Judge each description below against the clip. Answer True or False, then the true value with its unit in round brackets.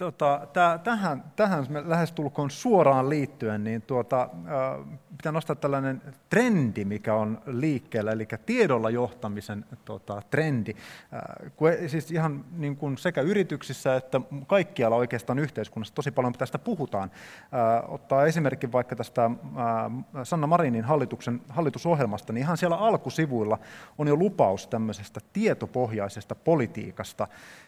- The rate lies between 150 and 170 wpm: False (115 wpm)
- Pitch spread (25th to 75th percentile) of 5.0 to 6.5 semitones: True (5.5 semitones)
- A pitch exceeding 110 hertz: True (135 Hz)